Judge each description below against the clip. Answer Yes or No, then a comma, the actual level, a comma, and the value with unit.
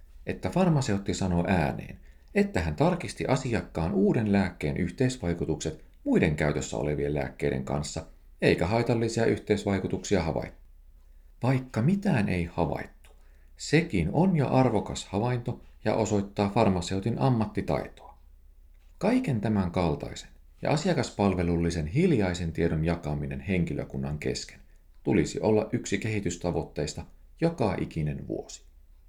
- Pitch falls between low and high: No, very low, 90 Hz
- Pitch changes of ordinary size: No, wide, 7.6 semitones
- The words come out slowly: No, average, 105 wpm